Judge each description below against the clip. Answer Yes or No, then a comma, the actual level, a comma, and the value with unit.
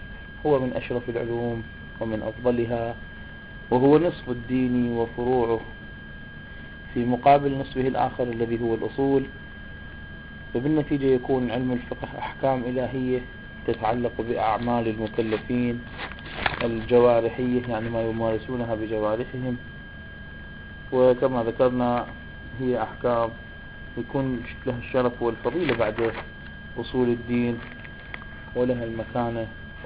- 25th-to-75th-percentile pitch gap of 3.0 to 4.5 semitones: No, narrow, 2.4 semitones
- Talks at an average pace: No, slow, 90 wpm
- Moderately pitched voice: No, low, 120 Hz